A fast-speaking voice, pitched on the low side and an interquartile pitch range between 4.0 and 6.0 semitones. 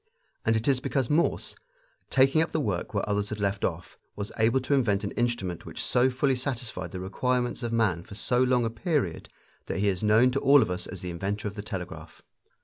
Yes: fast, 225 wpm; low, 115 Hz; average, 4.4 semitones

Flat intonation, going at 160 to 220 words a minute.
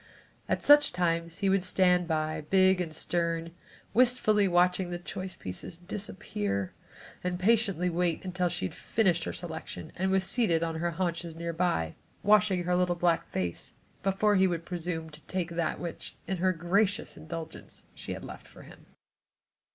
Yes: narrow, 2.2 semitones; average, 165 wpm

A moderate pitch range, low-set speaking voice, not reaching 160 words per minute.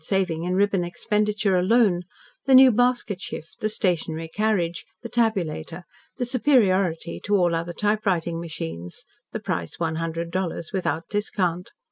No: average, 4.1 semitones; medium, 185 Hz; average, 140 wpm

